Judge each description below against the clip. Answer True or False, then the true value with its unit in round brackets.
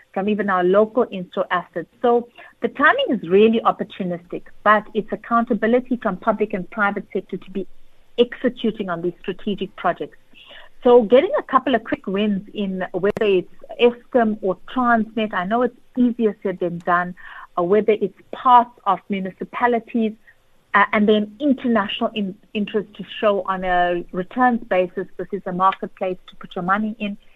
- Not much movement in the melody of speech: False (3.7 semitones)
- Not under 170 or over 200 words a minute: False (160 wpm)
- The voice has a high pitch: True (210 Hz)